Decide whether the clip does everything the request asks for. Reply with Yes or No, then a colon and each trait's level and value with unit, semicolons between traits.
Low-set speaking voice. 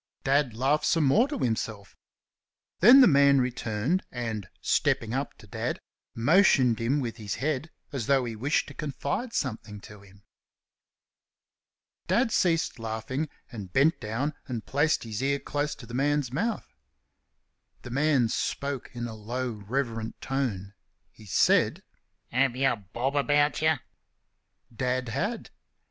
Yes: low, 130 Hz